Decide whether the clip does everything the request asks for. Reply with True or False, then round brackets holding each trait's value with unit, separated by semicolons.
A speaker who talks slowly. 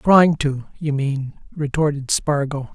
True (130 wpm)